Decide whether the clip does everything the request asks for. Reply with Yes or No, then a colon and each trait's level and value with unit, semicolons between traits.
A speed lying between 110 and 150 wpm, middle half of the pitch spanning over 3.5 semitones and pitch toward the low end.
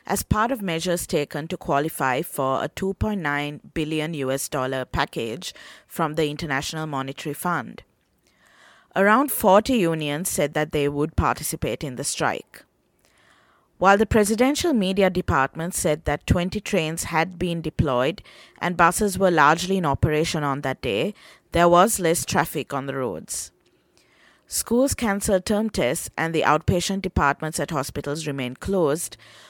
No: average, 140 wpm; average, 4.7 semitones; medium, 160 Hz